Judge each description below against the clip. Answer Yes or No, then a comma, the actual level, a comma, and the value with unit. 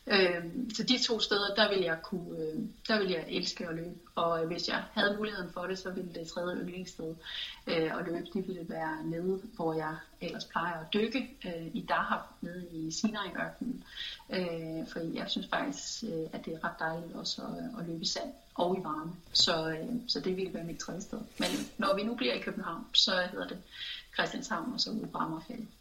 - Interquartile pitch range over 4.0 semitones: Yes, average, 4.6 semitones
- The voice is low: No, medium, 185 Hz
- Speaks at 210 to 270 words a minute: No, average, 190 wpm